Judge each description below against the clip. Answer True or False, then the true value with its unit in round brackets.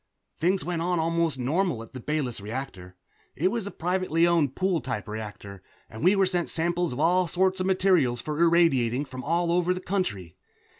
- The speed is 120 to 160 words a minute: False (190 wpm)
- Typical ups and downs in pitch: False (6.1 semitones)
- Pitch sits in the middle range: True (165 Hz)